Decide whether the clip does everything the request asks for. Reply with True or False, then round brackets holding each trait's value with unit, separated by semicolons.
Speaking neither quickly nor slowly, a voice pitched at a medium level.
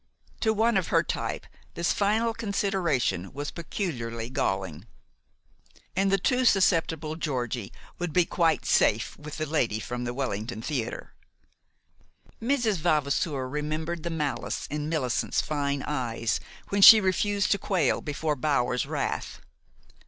False (130 wpm; 155 Hz)